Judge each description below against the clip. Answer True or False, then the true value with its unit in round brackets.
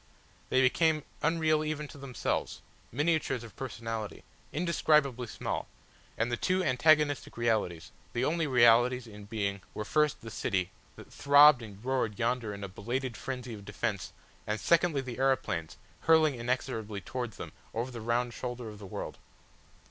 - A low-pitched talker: True (125 Hz)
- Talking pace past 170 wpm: False (155 wpm)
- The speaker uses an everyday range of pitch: True (4.4 semitones)